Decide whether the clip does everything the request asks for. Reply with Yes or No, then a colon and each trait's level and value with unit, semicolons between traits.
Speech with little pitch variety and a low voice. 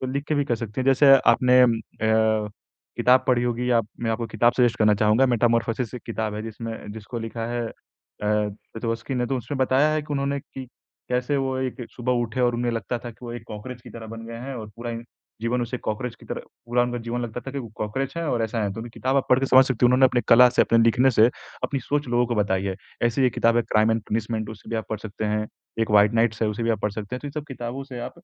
Yes: narrow, 2.3 semitones; low, 120 Hz